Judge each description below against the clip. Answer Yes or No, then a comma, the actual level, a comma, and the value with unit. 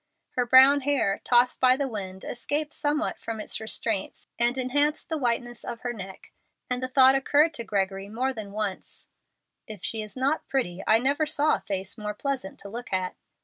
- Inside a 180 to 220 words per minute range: Yes, average, 190 wpm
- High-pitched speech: Yes, high, 240 Hz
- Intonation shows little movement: No, average, 4.5 semitones